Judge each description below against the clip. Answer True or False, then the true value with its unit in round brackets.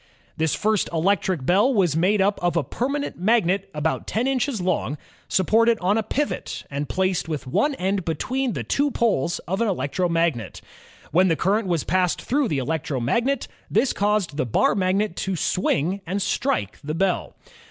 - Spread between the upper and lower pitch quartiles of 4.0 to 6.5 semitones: True (5.0 semitones)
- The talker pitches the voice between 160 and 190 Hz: True (185 Hz)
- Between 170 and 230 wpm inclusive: True (175 wpm)